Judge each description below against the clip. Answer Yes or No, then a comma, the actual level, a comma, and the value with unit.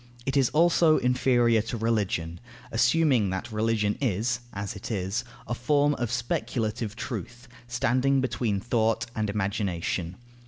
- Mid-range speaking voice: No, low, 115 Hz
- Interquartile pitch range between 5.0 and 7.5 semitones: No, average, 3.4 semitones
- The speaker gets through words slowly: Yes, slow, 130 wpm